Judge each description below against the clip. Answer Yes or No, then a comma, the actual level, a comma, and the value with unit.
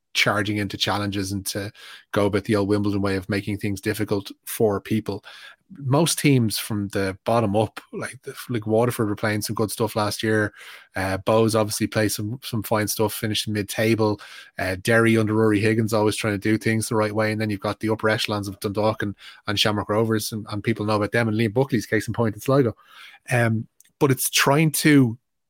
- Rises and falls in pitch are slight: Yes, narrow, 1.5 semitones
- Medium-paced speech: No, fast, 210 wpm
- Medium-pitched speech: No, low, 110 Hz